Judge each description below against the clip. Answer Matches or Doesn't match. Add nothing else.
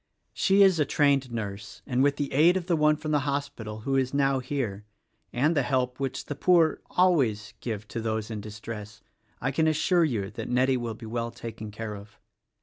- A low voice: Matches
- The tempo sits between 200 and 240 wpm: Matches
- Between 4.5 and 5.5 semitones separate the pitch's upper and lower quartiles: Matches